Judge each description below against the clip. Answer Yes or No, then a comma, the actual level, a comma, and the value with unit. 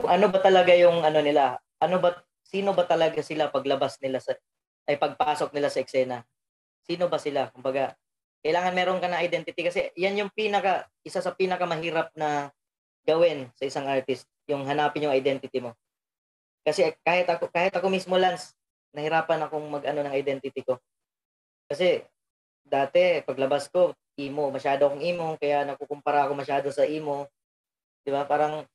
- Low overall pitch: No, medium, 150 Hz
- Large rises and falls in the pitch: No, average, 3.9 semitones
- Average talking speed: No, fast, 160 wpm